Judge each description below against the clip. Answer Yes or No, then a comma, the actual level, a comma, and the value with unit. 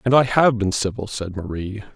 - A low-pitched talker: Yes, low, 110 Hz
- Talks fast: Yes, fast, 215 wpm